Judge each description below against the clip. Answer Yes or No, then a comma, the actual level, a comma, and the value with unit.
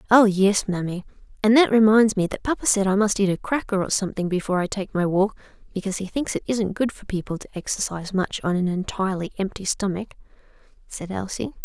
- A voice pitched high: Yes, high, 200 Hz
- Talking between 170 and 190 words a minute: No, fast, 205 wpm